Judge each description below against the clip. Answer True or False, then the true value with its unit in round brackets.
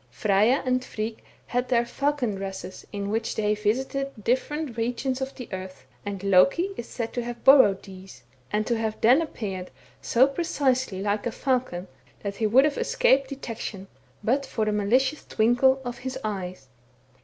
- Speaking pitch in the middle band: False (235 Hz)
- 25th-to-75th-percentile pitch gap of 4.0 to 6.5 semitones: True (4.5 semitones)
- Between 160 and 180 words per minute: True (165 wpm)